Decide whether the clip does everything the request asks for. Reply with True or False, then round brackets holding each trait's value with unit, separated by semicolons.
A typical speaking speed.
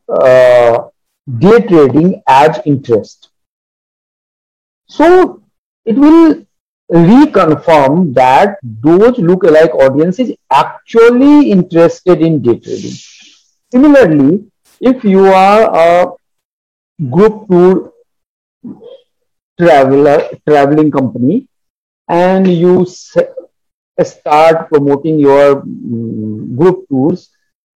False (80 wpm)